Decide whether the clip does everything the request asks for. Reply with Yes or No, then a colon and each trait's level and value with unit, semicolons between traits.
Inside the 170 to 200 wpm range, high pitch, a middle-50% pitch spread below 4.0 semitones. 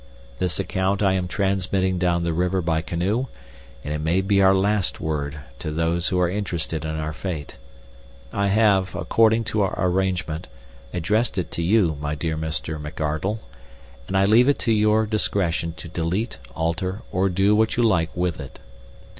No: average, 175 wpm; very low, 90 Hz; average, 3.6 semitones